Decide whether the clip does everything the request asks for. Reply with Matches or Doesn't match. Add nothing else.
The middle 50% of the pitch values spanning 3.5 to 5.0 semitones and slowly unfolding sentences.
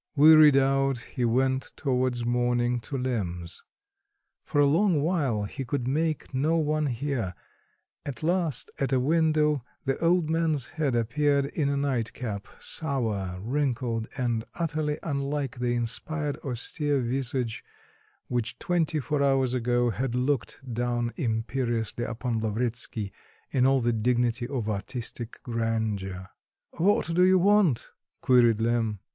Matches